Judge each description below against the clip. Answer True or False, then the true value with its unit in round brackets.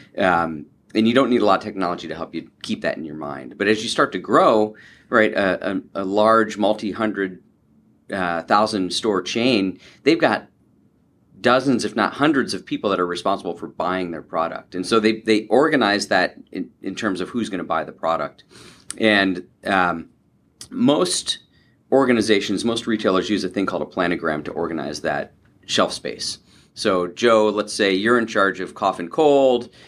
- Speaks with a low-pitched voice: True (105 Hz)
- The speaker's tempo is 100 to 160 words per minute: False (185 wpm)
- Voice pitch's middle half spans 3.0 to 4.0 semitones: True (3.3 semitones)